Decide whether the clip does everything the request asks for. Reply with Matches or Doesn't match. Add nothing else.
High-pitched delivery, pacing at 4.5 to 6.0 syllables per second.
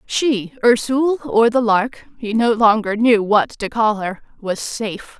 Doesn't match